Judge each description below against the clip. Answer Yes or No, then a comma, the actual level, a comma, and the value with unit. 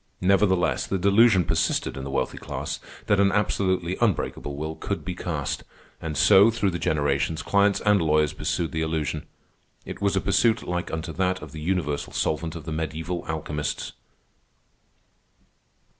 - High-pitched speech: No, very low, 85 Hz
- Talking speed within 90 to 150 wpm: No, average, 160 wpm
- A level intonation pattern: No, average, 3.9 semitones